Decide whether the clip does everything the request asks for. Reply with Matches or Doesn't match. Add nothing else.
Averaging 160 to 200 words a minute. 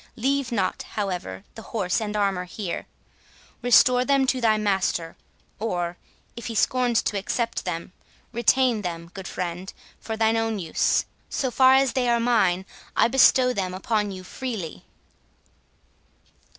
Doesn't match